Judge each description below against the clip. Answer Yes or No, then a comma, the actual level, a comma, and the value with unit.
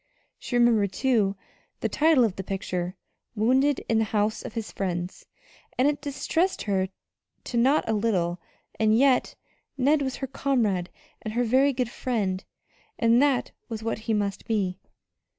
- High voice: Yes, high, 225 Hz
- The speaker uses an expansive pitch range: No, average, 4.7 semitones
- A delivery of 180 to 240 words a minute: No, average, 155 wpm